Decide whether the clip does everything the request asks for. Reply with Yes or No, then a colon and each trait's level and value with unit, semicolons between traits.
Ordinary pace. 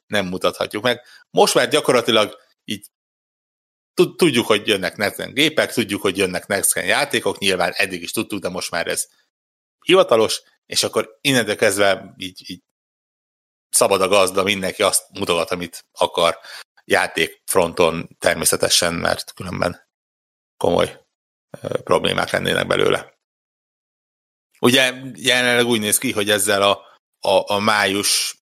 Yes: average, 125 wpm